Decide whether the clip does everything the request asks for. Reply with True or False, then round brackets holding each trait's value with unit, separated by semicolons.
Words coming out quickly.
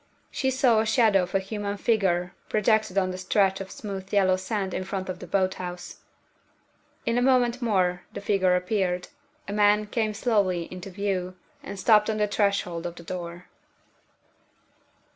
False (170 wpm)